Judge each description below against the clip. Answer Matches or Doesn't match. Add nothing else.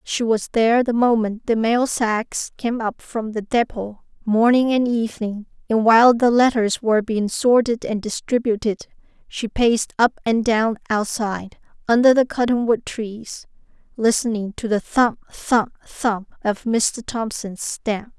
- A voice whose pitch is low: Doesn't match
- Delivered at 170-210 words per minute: Doesn't match